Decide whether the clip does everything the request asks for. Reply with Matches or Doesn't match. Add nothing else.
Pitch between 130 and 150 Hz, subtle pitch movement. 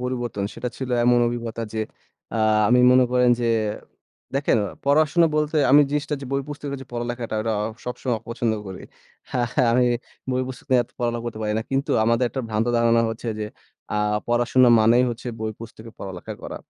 Doesn't match